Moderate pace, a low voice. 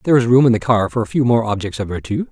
No: fast, 335 wpm; low, 115 Hz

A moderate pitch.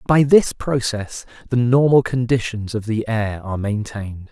No: low, 115 Hz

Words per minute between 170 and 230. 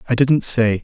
Yes: fast, 215 wpm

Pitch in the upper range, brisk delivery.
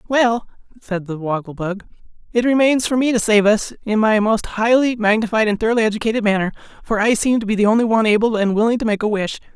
Yes: high, 220 Hz; fast, 225 wpm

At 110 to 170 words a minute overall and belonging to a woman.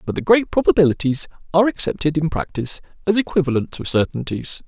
No: average, 155 wpm; male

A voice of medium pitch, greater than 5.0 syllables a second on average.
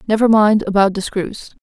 No: high, 205 Hz; 5.2 syllables/s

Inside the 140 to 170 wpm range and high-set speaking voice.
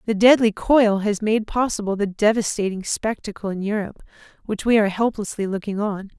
Yes: average, 165 wpm; high, 210 Hz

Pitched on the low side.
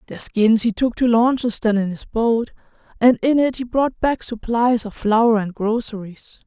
No: high, 230 Hz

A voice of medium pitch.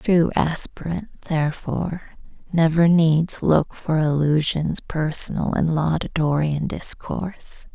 Yes: medium, 160 Hz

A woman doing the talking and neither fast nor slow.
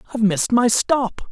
No: male; average, 185 wpm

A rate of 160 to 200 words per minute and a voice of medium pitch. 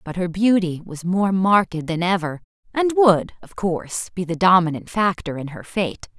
Yes: average, 185 wpm; medium, 180 Hz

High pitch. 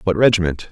No: very low, 95 Hz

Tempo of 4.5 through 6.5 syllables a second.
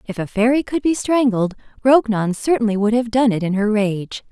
Yes: 5.2 syllables/s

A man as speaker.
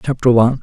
Yes: male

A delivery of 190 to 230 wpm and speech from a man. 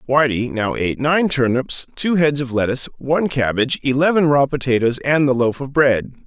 No: average, 180 wpm; male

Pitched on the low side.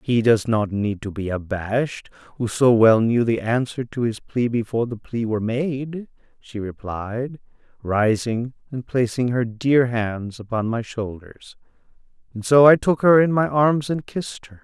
Yes: low, 120 Hz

